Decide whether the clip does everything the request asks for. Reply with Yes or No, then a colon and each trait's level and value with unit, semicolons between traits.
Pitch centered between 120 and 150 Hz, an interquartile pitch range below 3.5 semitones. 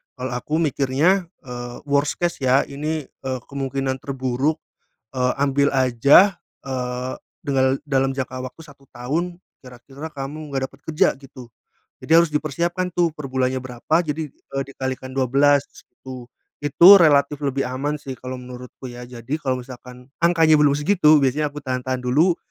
Yes: low, 135 Hz; average, 2.7 semitones